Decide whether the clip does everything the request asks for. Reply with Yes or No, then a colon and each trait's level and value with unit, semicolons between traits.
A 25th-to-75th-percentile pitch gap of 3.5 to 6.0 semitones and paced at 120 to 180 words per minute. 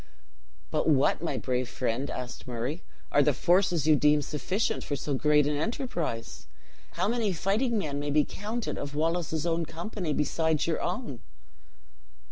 Yes: average, 3.8 semitones; average, 155 wpm